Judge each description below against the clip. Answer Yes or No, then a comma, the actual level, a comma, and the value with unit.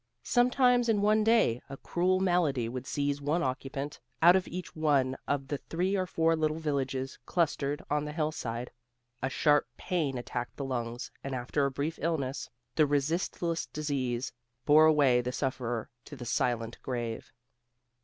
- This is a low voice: No, medium, 145 Hz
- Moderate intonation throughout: Yes, average, 4.1 semitones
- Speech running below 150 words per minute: No, average, 160 wpm